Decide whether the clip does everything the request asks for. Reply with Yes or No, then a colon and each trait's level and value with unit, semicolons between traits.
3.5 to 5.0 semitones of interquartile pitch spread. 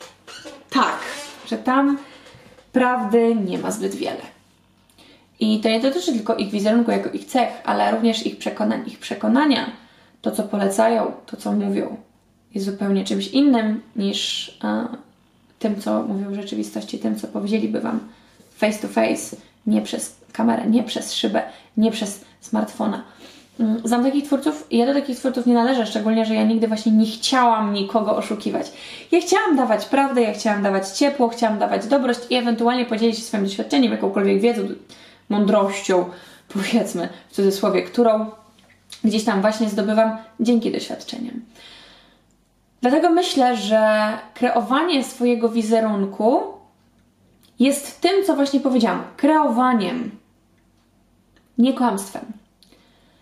No: average, 2.8 semitones